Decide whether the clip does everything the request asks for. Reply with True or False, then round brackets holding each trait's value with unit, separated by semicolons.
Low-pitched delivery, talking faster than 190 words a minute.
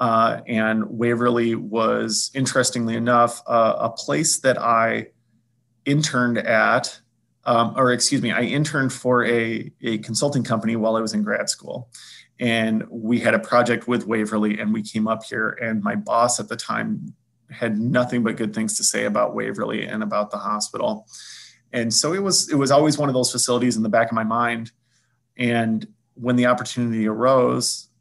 False (120 Hz; 180 wpm)